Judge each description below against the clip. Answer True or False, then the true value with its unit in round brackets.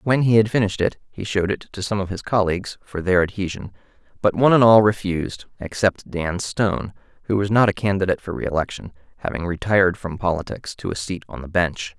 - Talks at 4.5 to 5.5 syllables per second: False (6.0 syllables/s)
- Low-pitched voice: True (95 Hz)